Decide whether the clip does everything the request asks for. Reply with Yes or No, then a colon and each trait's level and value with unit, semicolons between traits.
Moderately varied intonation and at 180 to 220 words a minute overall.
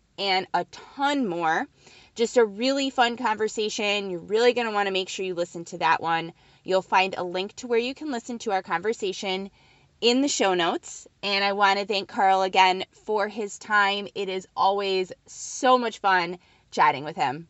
Yes: average, 3.5 semitones; average, 190 wpm